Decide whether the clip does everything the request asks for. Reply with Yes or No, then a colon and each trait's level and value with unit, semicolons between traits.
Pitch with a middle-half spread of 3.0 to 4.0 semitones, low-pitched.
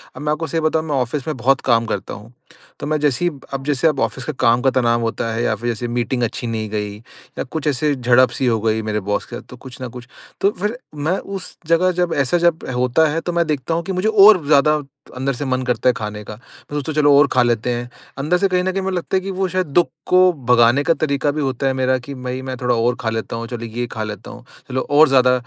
No: average, 4.8 semitones; low, 130 Hz